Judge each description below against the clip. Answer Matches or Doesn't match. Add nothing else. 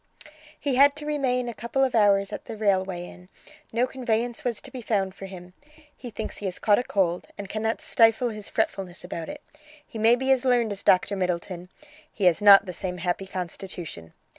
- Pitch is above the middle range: Matches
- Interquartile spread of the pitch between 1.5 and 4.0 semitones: Doesn't match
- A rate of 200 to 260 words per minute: Matches